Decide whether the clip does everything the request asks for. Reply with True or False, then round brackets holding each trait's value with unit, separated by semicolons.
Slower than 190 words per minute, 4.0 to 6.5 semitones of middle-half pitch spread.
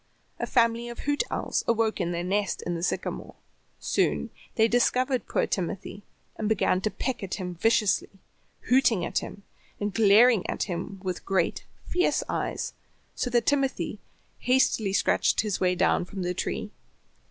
True (160 wpm; 4.4 semitones)